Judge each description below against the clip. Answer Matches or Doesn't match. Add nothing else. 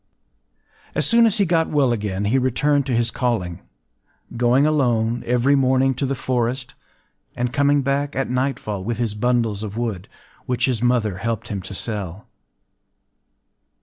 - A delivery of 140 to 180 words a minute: Matches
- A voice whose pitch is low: Matches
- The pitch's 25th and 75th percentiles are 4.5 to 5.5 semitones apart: Doesn't match